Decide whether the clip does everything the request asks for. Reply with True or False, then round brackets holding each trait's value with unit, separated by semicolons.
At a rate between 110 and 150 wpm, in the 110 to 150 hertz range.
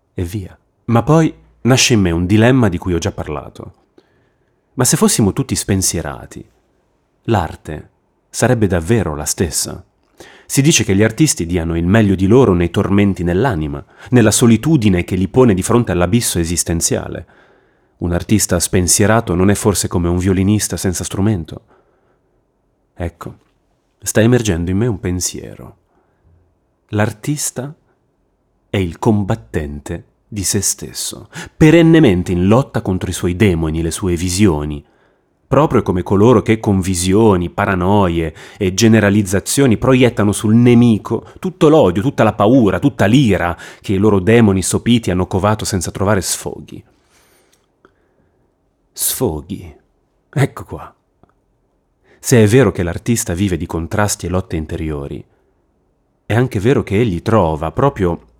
False (135 wpm; 100 Hz)